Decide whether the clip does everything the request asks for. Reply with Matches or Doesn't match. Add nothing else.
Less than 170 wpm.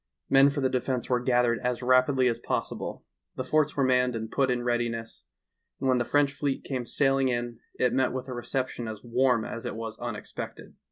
Doesn't match